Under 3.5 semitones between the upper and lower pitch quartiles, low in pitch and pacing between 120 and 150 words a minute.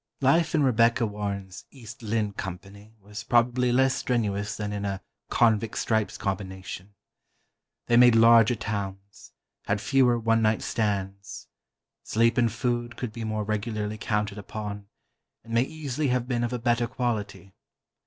Yes: average, 2.8 semitones; low, 110 Hz; average, 145 wpm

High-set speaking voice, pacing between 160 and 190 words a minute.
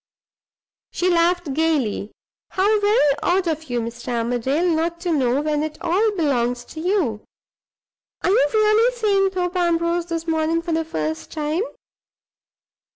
No: very high, 330 Hz; average, 145 wpm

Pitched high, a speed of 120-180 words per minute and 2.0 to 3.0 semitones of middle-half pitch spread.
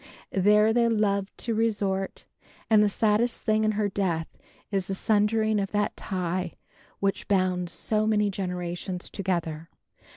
Yes: high, 200 Hz; average, 140 wpm; narrow, 2.6 semitones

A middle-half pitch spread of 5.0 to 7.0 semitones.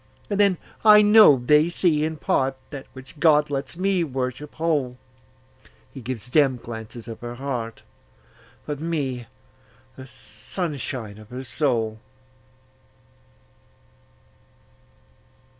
No: average, 3.8 semitones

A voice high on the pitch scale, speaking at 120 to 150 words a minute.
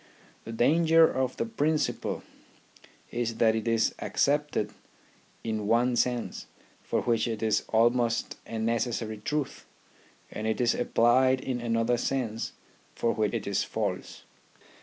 No: low, 120 Hz; slow, 135 wpm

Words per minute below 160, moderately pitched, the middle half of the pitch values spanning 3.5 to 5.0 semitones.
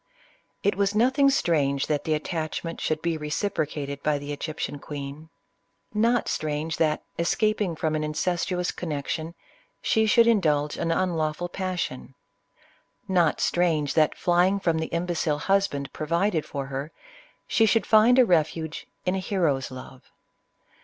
Yes: average, 150 wpm; medium, 165 Hz; average, 3.8 semitones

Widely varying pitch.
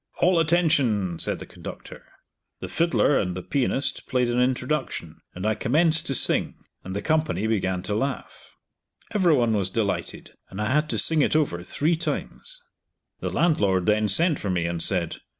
Yes: wide, 8.1 semitones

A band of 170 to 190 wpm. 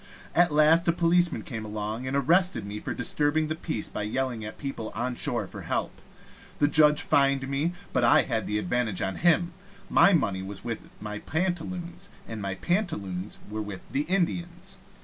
Yes: average, 175 wpm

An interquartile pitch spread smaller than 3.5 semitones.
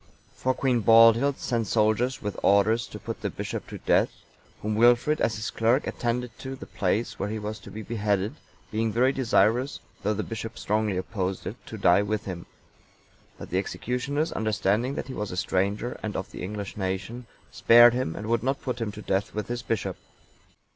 Yes: average, 2.9 semitones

